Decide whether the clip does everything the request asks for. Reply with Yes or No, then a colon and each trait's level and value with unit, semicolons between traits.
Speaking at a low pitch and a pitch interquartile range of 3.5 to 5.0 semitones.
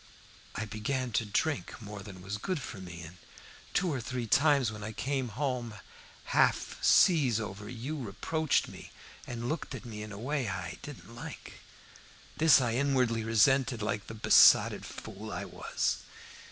Yes: low, 115 Hz; average, 4.4 semitones